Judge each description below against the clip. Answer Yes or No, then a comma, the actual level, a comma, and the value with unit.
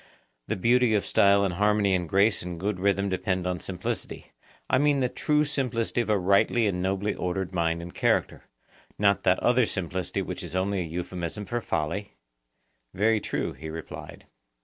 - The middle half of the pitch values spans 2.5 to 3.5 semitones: Yes, average, 3.1 semitones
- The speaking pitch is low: Yes, low, 100 Hz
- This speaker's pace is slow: No, average, 170 wpm